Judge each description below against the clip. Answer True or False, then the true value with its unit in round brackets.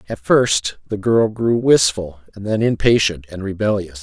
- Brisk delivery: False (165 wpm)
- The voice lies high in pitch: False (110 Hz)